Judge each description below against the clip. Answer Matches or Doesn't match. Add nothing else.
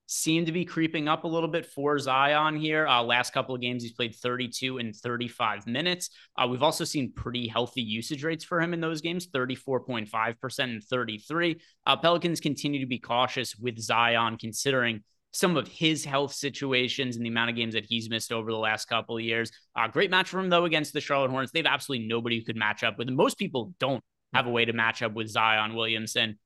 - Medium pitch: Doesn't match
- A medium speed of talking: Doesn't match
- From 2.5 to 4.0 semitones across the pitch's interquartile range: Doesn't match